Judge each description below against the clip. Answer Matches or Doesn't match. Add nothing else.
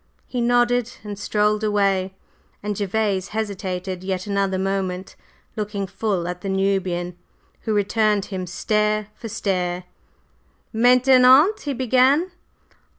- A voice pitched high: Matches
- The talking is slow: Matches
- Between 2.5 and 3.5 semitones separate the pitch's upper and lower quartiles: Matches